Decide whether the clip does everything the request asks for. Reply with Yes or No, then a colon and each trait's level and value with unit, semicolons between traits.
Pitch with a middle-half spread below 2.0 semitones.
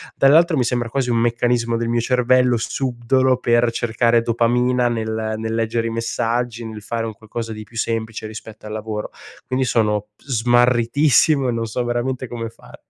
Yes: narrow, 1.6 semitones